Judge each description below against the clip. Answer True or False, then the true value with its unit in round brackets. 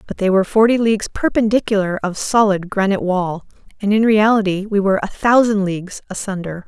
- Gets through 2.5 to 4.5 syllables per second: False (6.0 syllables/s)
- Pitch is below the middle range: False (205 Hz)